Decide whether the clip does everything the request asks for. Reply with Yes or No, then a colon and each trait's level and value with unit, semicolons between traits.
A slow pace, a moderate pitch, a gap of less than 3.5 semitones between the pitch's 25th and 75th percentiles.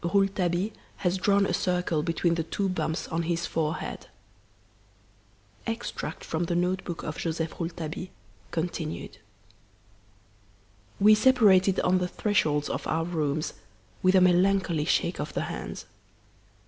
Yes: slow, 130 wpm; medium, 175 Hz; narrow, 2.6 semitones